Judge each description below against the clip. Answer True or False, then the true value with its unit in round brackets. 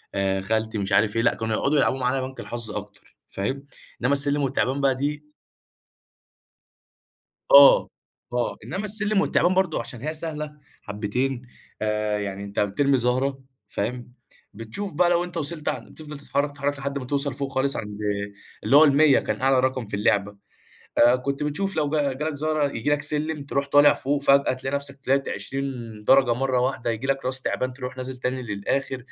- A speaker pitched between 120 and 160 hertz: True (135 Hz)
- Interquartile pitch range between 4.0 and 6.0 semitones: False (3.3 semitones)